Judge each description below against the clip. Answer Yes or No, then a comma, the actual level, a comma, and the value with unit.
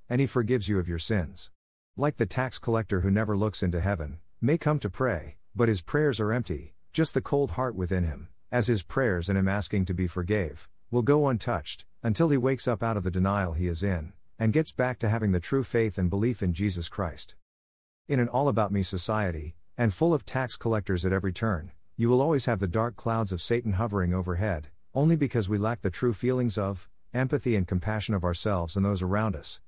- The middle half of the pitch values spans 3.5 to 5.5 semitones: Yes, average, 5.0 semitones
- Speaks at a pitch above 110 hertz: No, low, 105 Hz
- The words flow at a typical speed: No, fast, 220 wpm